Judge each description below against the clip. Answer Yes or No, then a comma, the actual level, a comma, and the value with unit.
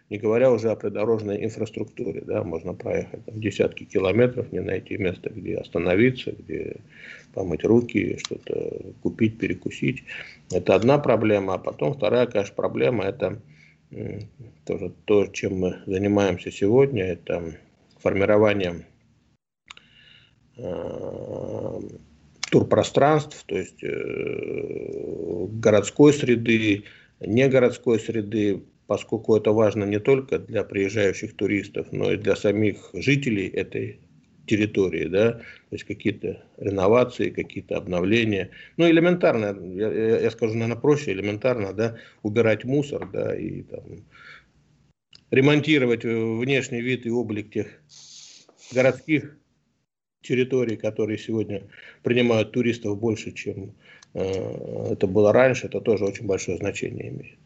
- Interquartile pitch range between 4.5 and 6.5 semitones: No, average, 3.9 semitones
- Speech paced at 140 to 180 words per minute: No, slow, 110 wpm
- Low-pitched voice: Yes, low, 115 Hz